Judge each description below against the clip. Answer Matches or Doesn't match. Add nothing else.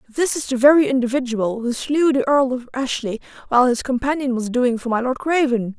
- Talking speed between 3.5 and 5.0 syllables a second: Doesn't match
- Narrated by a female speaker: Matches